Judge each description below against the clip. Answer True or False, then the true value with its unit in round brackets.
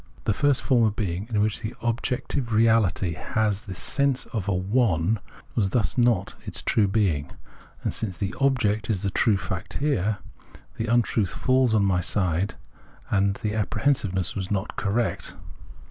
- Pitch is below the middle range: True (105 Hz)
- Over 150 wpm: True (165 wpm)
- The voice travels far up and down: False (3.4 semitones)